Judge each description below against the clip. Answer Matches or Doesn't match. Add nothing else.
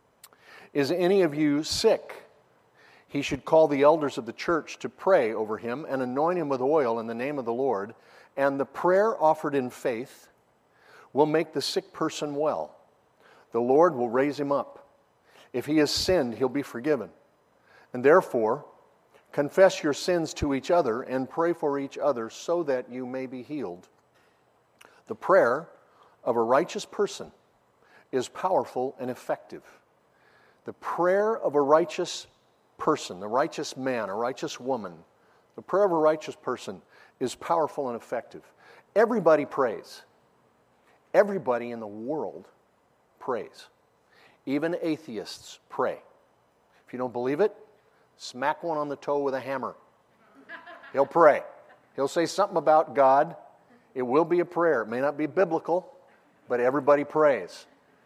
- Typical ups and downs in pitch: Matches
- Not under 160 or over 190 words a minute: Doesn't match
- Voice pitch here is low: Doesn't match